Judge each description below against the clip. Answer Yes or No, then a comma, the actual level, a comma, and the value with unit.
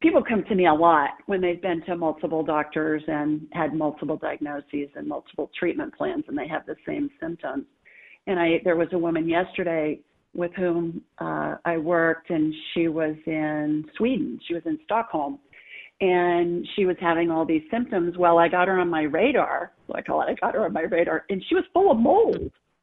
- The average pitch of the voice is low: No, medium, 170 Hz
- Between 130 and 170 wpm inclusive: No, average, 200 wpm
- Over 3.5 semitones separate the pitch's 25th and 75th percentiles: Yes, average, 4.7 semitones